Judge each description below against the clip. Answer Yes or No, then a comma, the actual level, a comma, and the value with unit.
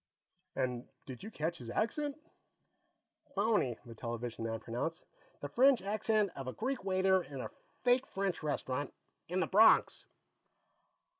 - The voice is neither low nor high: Yes, medium, 175 Hz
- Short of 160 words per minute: Yes, average, 140 wpm